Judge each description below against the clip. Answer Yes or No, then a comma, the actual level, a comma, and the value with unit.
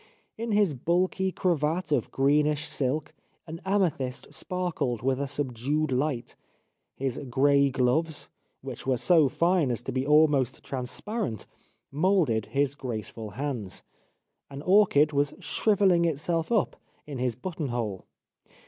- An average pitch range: Yes, average, 4.8 semitones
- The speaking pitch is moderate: Yes, medium, 145 Hz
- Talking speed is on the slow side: Yes, slow, 130 wpm